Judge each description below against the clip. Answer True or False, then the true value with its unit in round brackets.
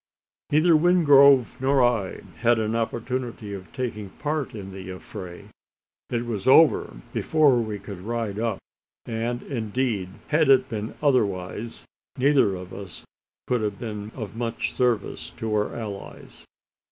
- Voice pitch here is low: True (115 Hz)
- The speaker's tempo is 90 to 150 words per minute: True (140 wpm)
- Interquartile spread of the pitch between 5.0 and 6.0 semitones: False (4.1 semitones)